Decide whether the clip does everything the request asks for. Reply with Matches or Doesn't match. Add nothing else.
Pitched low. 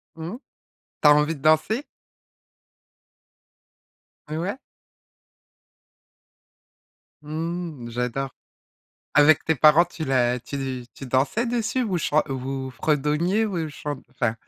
Doesn't match